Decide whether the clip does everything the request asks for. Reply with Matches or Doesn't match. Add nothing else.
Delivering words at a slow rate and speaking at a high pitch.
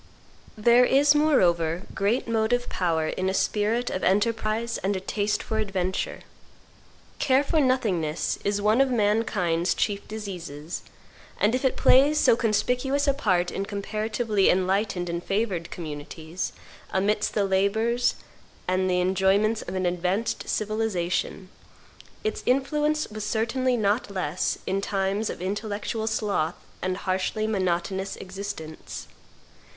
Matches